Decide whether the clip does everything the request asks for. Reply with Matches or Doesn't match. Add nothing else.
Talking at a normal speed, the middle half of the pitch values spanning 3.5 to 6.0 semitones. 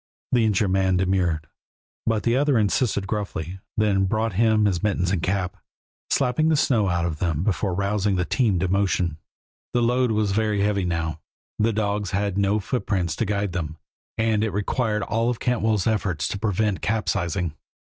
Doesn't match